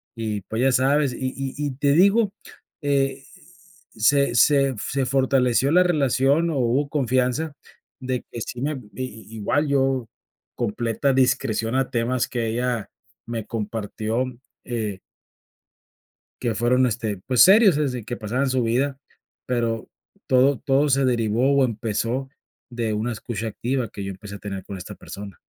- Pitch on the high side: No, low, 125 Hz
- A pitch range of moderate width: Yes, average, 3.3 semitones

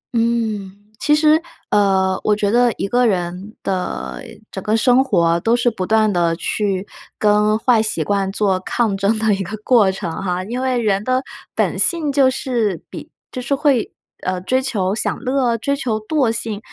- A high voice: Yes, high, 215 Hz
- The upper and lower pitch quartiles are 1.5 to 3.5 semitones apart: No, average, 4.2 semitones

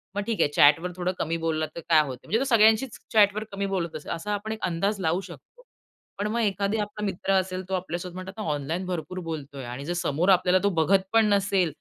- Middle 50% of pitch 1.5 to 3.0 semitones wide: No, average, 3.8 semitones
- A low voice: No, medium, 185 Hz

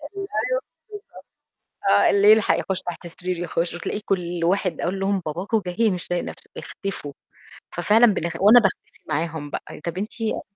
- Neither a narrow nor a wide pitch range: Yes, average, 3.3 semitones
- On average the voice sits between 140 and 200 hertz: Yes, medium, 185 Hz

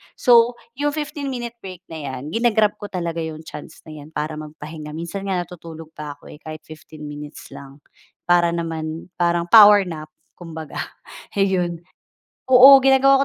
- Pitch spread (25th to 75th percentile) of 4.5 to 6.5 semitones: Yes, average, 5.0 semitones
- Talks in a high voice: No, medium, 170 Hz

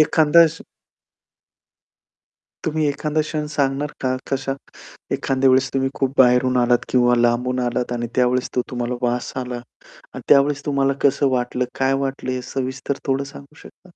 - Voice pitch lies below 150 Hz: Yes, low, 135 Hz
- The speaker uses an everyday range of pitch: No, narrow, 2.0 semitones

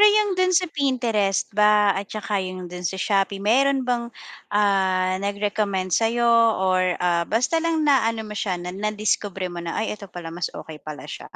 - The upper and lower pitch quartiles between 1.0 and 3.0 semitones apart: No, average, 3.9 semitones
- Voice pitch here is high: Yes, high, 205 Hz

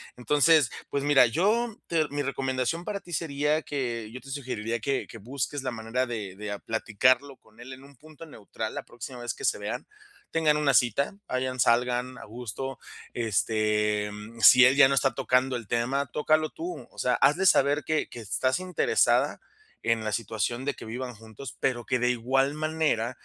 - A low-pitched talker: Yes, low, 130 Hz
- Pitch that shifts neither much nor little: Yes, average, 3.7 semitones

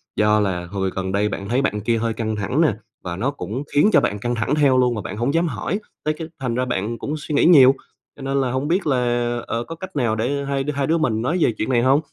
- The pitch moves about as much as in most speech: Yes, average, 4.8 semitones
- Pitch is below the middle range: Yes, low, 125 Hz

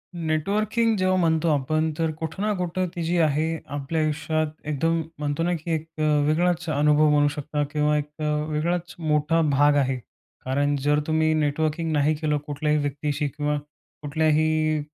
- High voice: No, medium, 155 Hz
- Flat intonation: Yes, narrow, 1.8 semitones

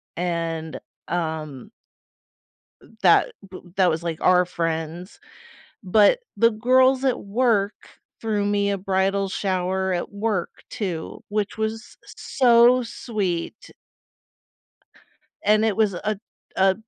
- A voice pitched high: Yes, high, 195 Hz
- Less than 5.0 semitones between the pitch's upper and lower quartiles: Yes, average, 3.6 semitones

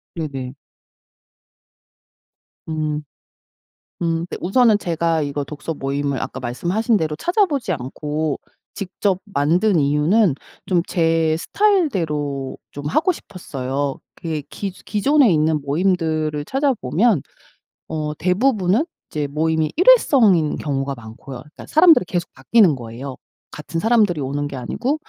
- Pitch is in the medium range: Yes, medium, 160 Hz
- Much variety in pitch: Yes, wide, 6.1 semitones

